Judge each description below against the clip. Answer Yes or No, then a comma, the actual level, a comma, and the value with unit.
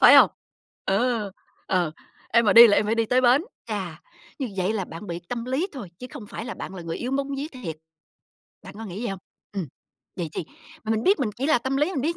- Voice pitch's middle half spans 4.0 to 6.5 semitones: Yes, average, 5.1 semitones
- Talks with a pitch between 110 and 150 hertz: No, high, 230 Hz